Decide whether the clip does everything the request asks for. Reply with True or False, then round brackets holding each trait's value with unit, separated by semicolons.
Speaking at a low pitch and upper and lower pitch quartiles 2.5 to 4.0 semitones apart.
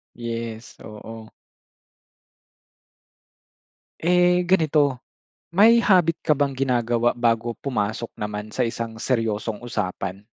False (120 Hz; 4.5 semitones)